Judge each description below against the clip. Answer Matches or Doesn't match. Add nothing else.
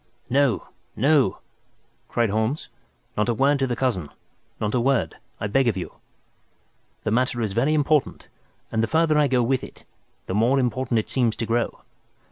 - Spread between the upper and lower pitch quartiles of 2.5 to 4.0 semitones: Matches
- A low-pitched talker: Matches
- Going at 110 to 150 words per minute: Doesn't match